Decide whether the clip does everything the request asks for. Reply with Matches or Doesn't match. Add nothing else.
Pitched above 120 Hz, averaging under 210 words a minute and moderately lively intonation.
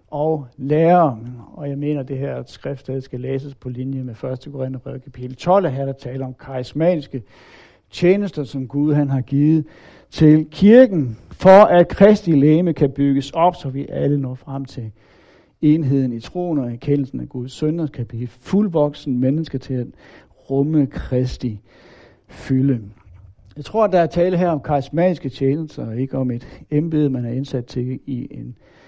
Matches